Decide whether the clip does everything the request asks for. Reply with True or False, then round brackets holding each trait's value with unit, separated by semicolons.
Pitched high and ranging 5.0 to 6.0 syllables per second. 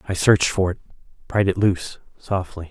False (95 Hz; 5.8 syllables/s)